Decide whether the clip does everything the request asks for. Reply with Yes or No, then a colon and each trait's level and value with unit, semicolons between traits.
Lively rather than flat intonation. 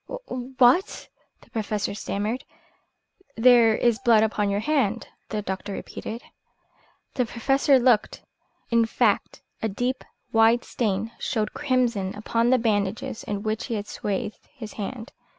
No: average, 2.8 semitones